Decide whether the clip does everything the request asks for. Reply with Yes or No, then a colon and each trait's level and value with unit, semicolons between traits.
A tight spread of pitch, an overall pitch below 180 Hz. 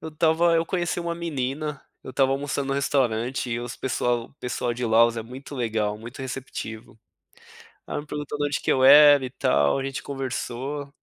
No: average, 3.4 semitones; low, 135 Hz